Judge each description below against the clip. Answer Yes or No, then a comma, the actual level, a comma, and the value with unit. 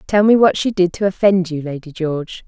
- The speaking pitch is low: No, medium, 180 Hz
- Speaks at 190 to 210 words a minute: No, fast, 240 wpm